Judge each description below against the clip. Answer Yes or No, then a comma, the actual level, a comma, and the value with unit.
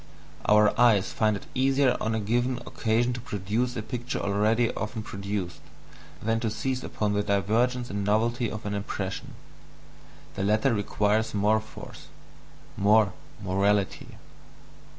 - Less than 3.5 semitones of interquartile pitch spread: Yes, average, 2.8 semitones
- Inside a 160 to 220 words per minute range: No, slow, 135 wpm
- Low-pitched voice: Yes, low, 110 Hz